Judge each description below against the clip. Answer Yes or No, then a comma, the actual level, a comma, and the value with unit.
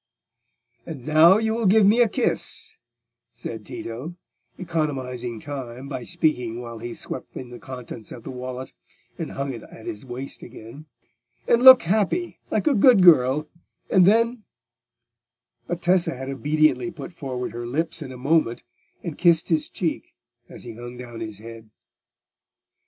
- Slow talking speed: No, average, 155 wpm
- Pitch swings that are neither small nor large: No, wide, 6.2 semitones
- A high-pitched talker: No, medium, 140 Hz